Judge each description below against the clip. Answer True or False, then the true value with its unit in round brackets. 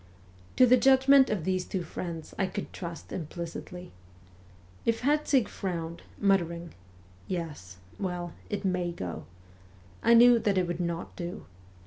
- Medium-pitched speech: True (180 Hz)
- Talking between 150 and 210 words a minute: False (140 wpm)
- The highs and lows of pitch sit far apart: False (4.0 semitones)